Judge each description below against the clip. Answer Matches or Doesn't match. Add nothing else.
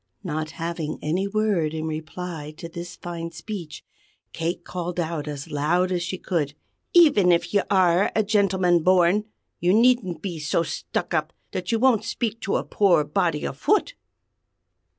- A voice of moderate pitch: Matches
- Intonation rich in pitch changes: Doesn't match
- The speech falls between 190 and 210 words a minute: Doesn't match